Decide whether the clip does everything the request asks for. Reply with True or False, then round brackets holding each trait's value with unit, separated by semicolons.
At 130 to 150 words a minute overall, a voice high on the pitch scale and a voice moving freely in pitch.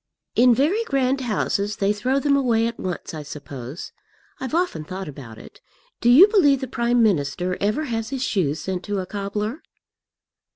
False (175 wpm; 220 Hz; 6.2 semitones)